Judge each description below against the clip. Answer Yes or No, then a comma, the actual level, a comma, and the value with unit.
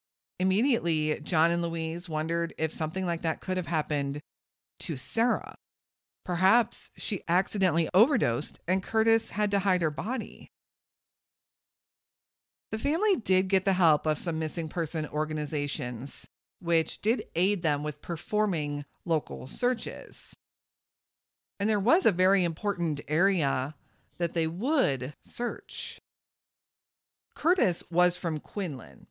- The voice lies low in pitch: No, medium, 170 Hz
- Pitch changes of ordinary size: Yes, average, 4.3 semitones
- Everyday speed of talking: No, slow, 120 wpm